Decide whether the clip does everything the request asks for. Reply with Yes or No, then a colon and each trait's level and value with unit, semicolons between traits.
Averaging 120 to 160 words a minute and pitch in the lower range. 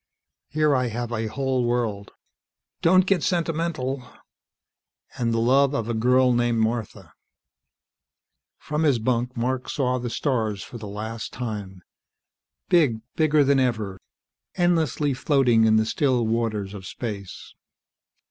Yes: average, 140 wpm; low, 120 Hz